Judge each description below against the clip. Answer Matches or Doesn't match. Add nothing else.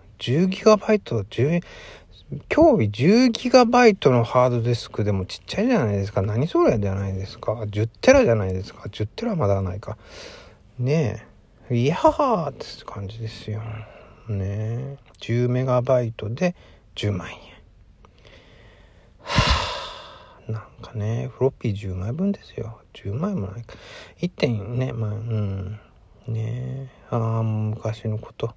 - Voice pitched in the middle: Doesn't match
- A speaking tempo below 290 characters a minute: Matches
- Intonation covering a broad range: Doesn't match